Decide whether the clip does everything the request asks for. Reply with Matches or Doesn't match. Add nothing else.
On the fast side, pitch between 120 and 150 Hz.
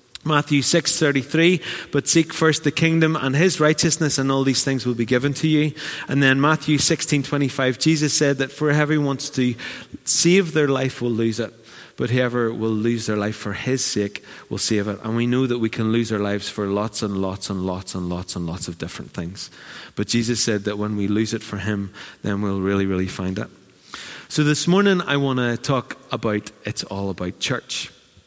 Matches